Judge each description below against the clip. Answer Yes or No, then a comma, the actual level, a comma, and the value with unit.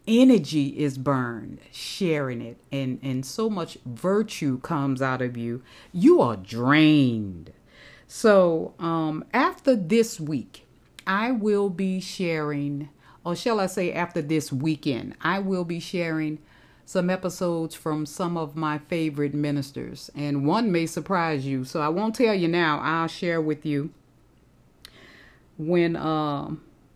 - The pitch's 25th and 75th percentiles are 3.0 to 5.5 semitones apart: Yes, average, 4.2 semitones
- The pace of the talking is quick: No, average, 140 wpm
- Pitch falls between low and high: Yes, medium, 155 Hz